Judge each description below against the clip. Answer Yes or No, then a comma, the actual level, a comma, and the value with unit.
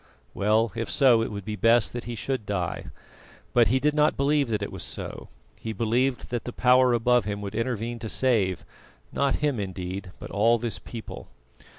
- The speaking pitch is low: Yes, low, 115 Hz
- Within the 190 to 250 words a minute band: Yes, average, 195 wpm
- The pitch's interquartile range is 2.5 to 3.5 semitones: Yes, average, 3.2 semitones